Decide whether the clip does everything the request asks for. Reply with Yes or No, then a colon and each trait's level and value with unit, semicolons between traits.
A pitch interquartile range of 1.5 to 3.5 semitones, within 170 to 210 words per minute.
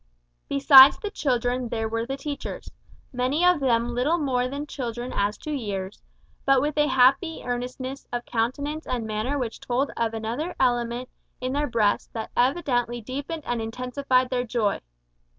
No: average, 3.0 semitones; average, 160 wpm